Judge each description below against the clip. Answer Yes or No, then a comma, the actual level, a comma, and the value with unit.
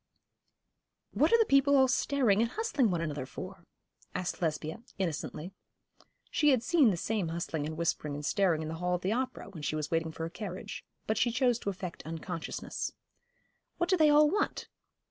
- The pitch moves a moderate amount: No, wide, 8.0 semitones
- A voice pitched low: No, high, 190 Hz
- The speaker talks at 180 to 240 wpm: Yes, average, 190 wpm